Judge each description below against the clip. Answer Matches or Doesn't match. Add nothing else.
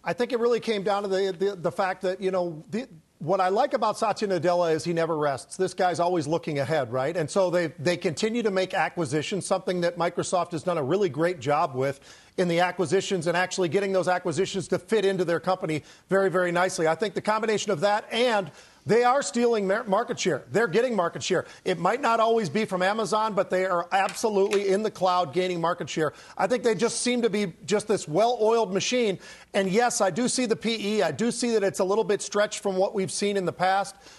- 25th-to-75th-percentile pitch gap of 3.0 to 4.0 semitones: Matches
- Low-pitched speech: Doesn't match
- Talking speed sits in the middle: Doesn't match